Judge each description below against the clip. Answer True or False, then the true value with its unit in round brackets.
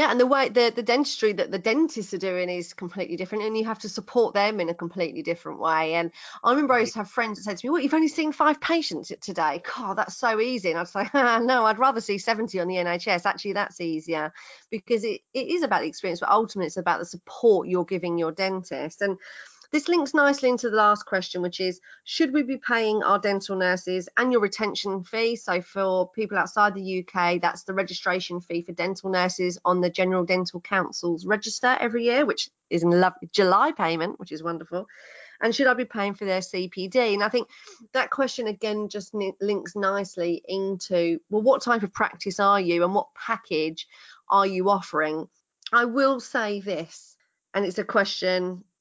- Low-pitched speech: False (200 Hz)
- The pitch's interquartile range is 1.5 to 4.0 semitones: False (4.4 semitones)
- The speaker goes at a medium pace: False (210 wpm)